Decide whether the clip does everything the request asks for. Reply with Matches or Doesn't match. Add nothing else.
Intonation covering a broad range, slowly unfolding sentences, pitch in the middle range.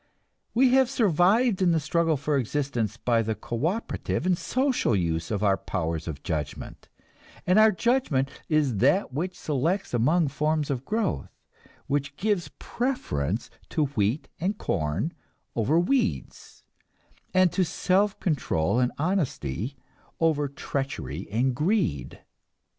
Matches